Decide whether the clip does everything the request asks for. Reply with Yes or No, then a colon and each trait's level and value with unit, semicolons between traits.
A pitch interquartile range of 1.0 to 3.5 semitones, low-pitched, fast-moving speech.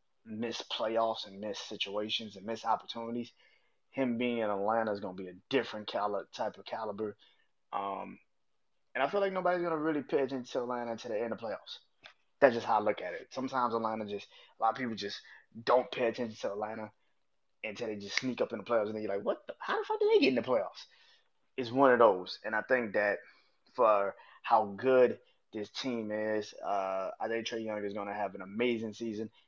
Yes: average, 2.8 semitones; low, 115 Hz; fast, 220 wpm